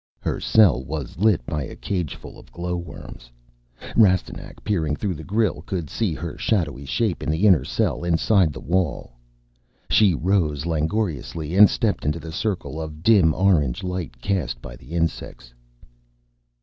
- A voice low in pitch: Yes, very low, 85 Hz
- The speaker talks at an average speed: Yes, average, 150 wpm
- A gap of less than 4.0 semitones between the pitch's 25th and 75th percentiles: No, average, 4.3 semitones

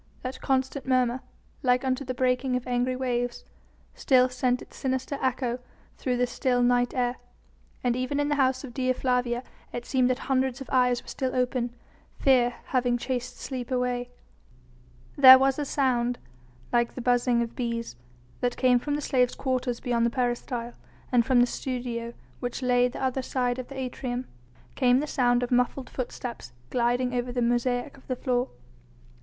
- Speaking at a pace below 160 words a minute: No, average, 175 wpm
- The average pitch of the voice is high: Yes, very high, 250 Hz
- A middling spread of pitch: No, narrow, 1.1 semitones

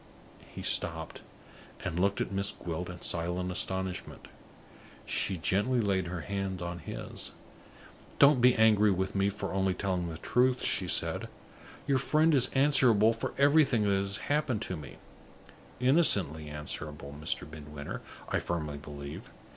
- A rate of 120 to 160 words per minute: Yes, average, 145 wpm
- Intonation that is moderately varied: No, wide, 5.7 semitones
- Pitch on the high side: No, very low, 95 Hz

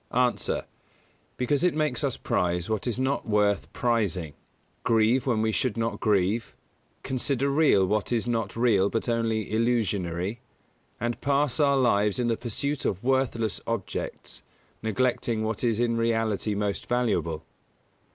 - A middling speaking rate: Yes, average, 145 wpm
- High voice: No, low, 115 Hz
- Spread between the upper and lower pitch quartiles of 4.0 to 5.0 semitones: No, average, 3.0 semitones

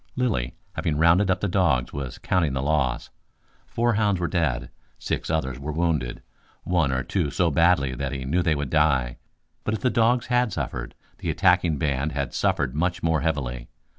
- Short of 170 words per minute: No, average, 185 wpm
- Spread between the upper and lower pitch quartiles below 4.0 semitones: No, average, 5.1 semitones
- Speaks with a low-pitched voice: Yes, very low, 80 Hz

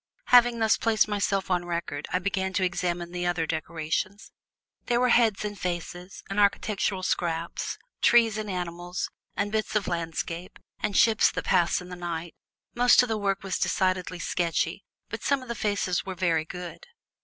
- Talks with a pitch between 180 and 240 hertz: Yes, medium, 185 Hz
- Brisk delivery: No, average, 175 wpm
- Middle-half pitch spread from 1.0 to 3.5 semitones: Yes, average, 3.2 semitones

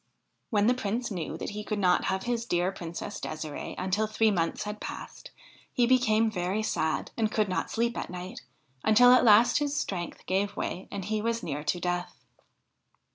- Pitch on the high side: Yes, high, 210 Hz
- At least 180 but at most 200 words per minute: Yes, average, 185 wpm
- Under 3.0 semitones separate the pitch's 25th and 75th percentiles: No, average, 3.9 semitones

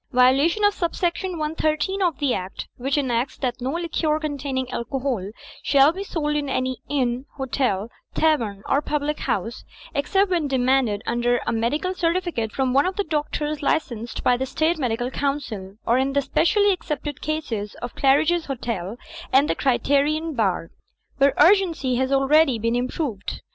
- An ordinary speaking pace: Yes, average, 165 wpm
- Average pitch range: Yes, average, 4.2 semitones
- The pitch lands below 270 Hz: No, very high, 275 Hz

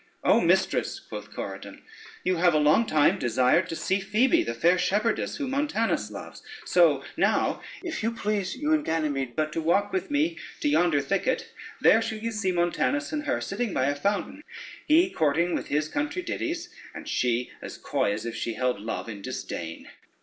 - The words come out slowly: No, average, 185 wpm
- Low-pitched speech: No, high, 190 Hz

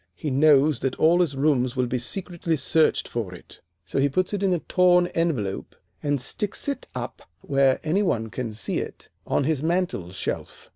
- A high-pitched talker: No, medium, 145 Hz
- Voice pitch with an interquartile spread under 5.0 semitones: No, wide, 5.4 semitones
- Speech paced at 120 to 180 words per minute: No, average, 190 wpm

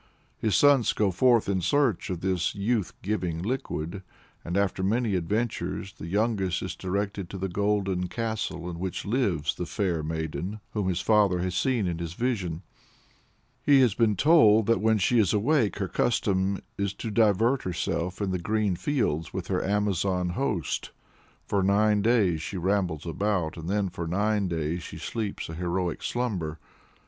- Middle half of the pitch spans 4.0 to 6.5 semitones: No, average, 3.5 semitones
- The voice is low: Yes, low, 100 Hz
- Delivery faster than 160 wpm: Yes, average, 170 wpm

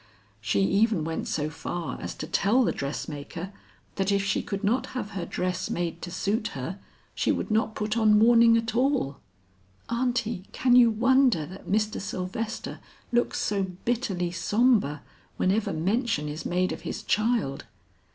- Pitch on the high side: Yes, high, 205 Hz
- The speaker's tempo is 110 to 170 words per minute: Yes, average, 160 wpm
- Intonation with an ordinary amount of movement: Yes, average, 4.6 semitones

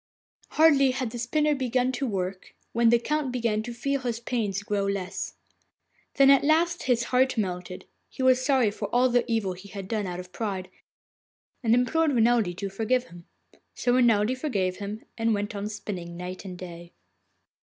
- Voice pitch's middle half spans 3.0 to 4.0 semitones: No, average, 4.5 semitones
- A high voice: Yes, high, 225 Hz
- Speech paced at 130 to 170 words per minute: No, average, 180 wpm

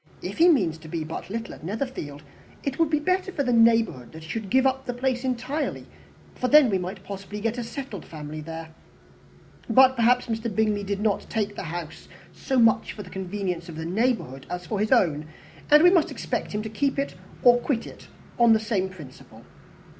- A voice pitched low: No, high, 220 Hz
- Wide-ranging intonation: Yes, wide, 6.0 semitones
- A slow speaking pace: No, fast, 205 wpm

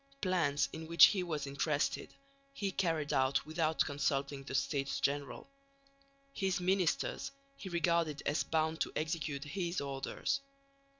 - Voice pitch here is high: No, medium, 155 Hz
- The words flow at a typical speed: No, slow, 130 wpm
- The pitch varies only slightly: No, average, 3.5 semitones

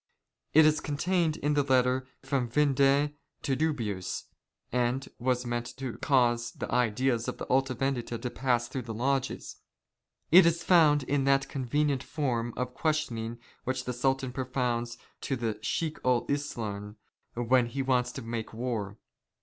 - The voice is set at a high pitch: No, low, 130 Hz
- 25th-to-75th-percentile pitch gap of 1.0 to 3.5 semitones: Yes, average, 2.8 semitones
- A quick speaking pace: No, average, 155 wpm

